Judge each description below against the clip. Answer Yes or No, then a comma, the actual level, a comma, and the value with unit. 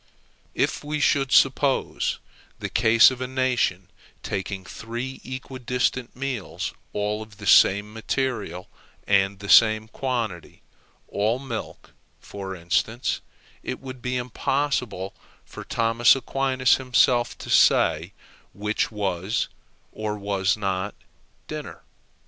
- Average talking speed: No, slow, 115 wpm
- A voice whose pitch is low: Yes, low, 115 Hz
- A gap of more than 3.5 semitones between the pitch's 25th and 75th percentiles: Yes, average, 4.1 semitones